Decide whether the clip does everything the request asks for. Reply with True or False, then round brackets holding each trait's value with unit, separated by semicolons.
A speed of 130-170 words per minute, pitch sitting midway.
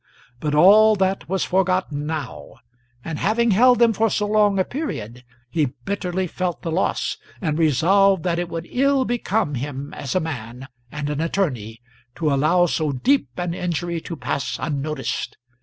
True (165 wpm; 170 Hz)